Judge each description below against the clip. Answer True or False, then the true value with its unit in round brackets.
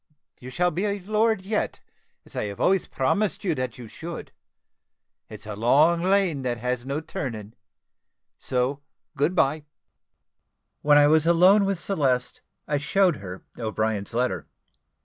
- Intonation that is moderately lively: False (6.5 semitones)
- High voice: False (145 Hz)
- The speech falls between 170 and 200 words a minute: False (145 wpm)